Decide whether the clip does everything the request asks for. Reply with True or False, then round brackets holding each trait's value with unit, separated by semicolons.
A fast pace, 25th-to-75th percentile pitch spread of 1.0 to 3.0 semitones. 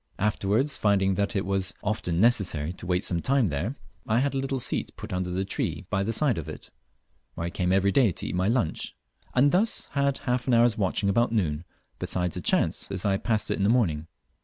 False (230 wpm; 4.8 semitones)